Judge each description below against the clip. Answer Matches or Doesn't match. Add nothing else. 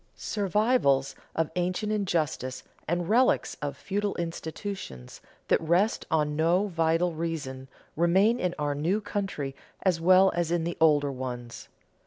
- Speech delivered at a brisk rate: Doesn't match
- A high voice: Doesn't match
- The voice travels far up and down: Doesn't match